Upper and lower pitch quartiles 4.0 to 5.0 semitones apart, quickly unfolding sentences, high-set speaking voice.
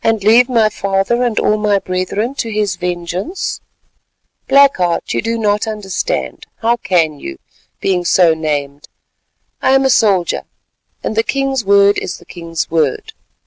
No: average, 4.5 semitones; average, 155 wpm; high, 200 Hz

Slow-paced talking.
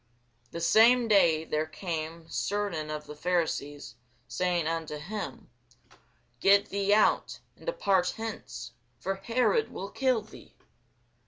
Yes: slow, 120 wpm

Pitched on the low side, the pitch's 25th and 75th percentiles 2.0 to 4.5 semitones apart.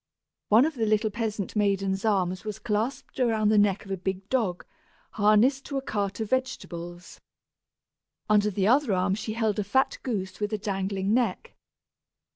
No: high, 210 Hz; narrow, 2.6 semitones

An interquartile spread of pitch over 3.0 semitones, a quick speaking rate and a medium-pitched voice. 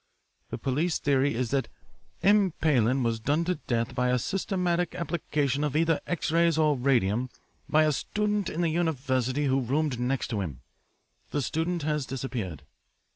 No: average, 4.6 semitones; average, 165 wpm; medium, 145 Hz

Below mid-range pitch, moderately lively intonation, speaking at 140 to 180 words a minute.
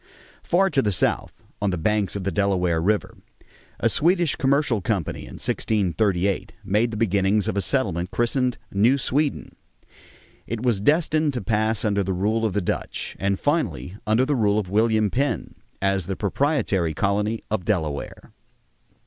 Yes: low, 105 Hz; average, 4.1 semitones; average, 160 wpm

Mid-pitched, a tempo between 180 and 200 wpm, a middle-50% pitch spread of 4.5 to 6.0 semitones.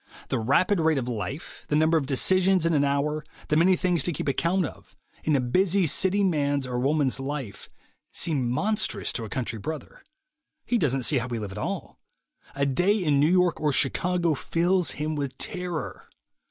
Yes: medium, 150 Hz; average, 190 wpm; average, 4.9 semitones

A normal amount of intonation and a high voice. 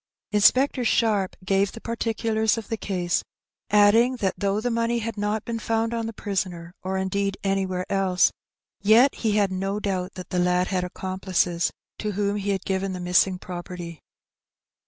Yes: average, 3.0 semitones; high, 200 Hz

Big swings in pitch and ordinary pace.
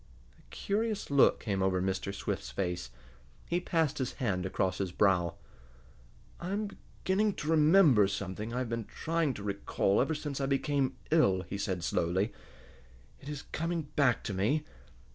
Yes: wide, 8.3 semitones; average, 160 wpm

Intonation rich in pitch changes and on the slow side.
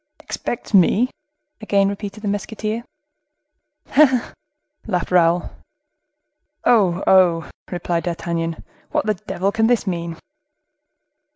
No: average, 3.8 semitones; slow, 110 wpm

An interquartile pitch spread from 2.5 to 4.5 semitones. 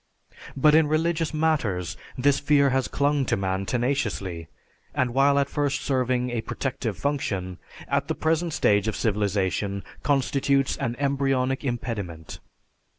No: wide, 5.4 semitones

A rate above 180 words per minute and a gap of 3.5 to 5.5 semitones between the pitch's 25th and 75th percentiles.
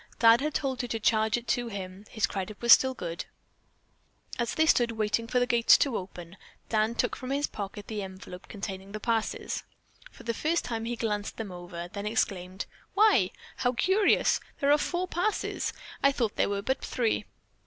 Yes: average, 190 wpm; average, 4.0 semitones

